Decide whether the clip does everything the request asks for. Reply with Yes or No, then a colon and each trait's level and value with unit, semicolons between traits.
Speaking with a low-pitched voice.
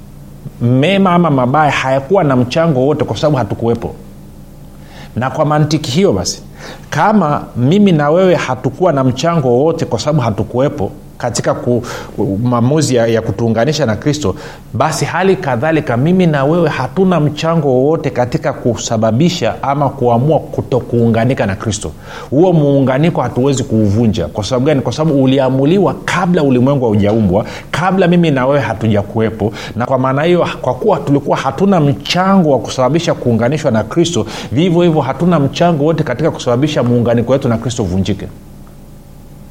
Yes: low, 130 Hz